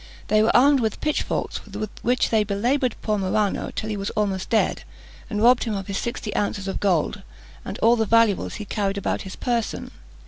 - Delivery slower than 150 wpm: No, average, 200 wpm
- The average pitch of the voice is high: Yes, high, 215 Hz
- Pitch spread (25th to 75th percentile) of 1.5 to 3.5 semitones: Yes, narrow, 2.6 semitones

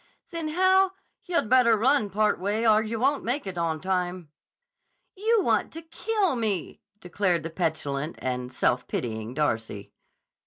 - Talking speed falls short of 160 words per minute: Yes, average, 150 wpm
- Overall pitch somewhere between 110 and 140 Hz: No, high, 205 Hz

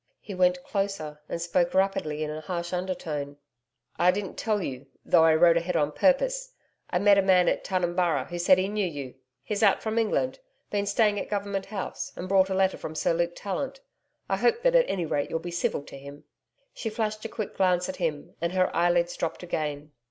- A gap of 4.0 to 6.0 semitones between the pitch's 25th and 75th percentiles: No, average, 3.4 semitones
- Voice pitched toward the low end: No, medium, 180 Hz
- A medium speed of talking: No, fast, 210 wpm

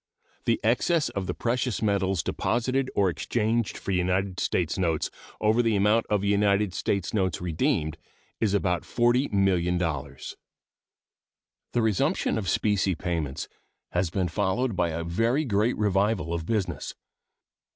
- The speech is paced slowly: Yes, slow, 130 wpm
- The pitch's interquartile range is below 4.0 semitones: No, average, 4.3 semitones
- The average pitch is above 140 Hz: No, low, 100 Hz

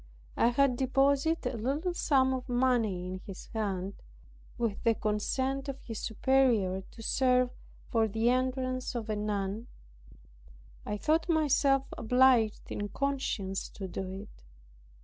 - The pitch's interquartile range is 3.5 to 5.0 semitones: Yes, average, 4.2 semitones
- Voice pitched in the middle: No, high, 245 Hz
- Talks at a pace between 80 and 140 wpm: Yes, slow, 135 wpm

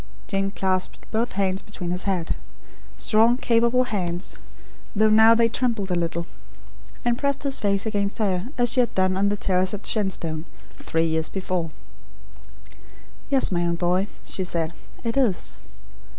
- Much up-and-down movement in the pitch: No, average, 4.1 semitones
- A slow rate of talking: No, average, 155 wpm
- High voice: Yes, high, 195 Hz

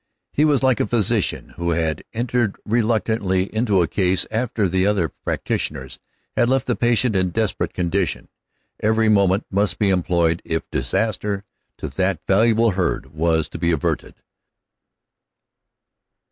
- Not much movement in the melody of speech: No, average, 4.4 semitones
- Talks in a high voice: No, low, 100 Hz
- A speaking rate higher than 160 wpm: No, slow, 135 wpm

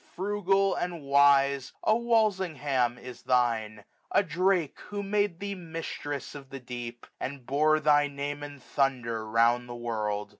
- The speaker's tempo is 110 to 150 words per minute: Yes, average, 145 wpm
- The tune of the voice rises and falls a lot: Yes, wide, 6.5 semitones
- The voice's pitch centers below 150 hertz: Yes, medium, 140 Hz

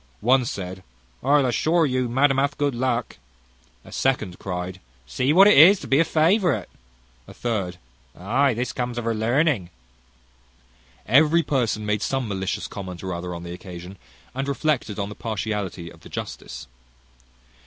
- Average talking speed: Yes, average, 165 wpm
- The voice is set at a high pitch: No, low, 120 Hz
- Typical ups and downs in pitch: No, wide, 6.5 semitones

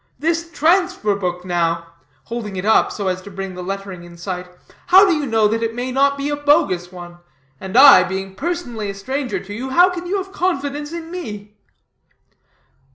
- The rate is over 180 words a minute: Yes, average, 195 wpm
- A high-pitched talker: Yes, high, 225 Hz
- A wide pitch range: Yes, wide, 7.9 semitones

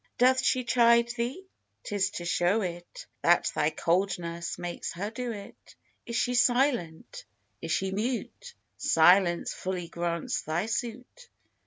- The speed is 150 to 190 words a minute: No, slow, 135 wpm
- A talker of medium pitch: No, high, 200 Hz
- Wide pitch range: Yes, wide, 5.8 semitones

